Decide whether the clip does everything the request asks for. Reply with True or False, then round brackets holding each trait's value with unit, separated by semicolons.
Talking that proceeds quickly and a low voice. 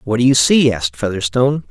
True (210 wpm; 125 Hz)